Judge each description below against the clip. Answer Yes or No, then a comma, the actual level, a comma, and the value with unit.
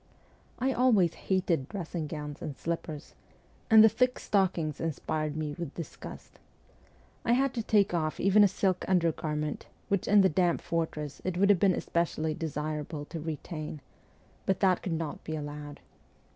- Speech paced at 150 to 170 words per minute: Yes, average, 160 wpm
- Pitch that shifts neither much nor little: Yes, average, 4.0 semitones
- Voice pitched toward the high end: No, medium, 165 Hz